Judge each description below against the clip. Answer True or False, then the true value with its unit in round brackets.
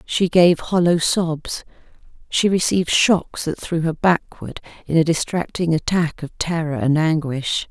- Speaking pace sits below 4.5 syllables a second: True (4.2 syllables/s)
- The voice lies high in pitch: False (165 Hz)